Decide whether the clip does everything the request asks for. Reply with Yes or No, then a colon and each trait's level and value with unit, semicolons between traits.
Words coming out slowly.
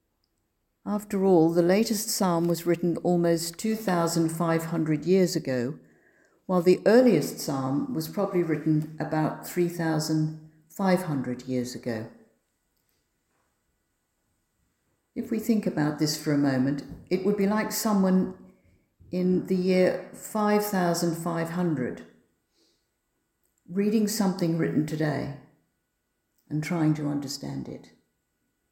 Yes: slow, 100 wpm